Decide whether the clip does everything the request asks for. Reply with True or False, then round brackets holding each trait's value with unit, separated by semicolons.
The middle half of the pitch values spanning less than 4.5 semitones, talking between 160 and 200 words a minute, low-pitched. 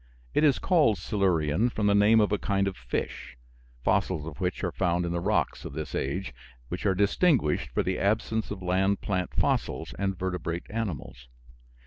True (3.1 semitones; 180 wpm; 95 Hz)